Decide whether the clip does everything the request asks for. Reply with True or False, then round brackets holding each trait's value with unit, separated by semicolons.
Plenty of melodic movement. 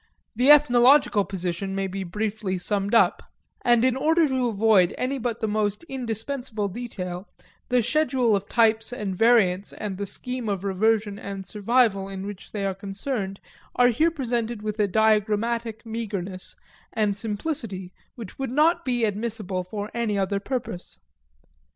False (3.6 semitones)